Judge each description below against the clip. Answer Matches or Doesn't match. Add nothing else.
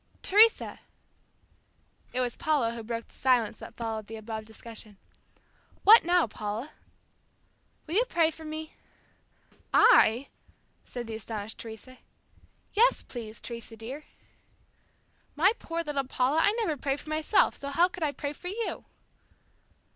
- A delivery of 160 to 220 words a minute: Doesn't match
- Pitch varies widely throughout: Matches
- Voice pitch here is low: Doesn't match